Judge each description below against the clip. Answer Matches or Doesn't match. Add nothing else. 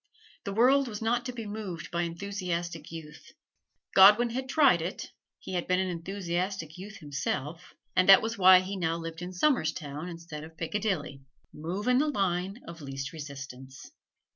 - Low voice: Doesn't match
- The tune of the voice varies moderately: Matches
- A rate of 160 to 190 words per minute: Matches